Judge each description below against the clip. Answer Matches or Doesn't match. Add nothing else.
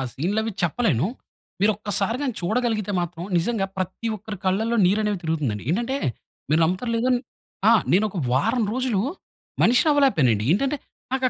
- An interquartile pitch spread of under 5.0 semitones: Doesn't match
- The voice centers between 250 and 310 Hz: Doesn't match